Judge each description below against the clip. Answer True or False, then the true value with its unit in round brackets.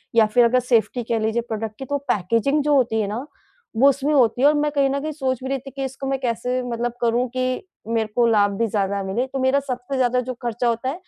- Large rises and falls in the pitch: False (2.9 semitones)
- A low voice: False (250 Hz)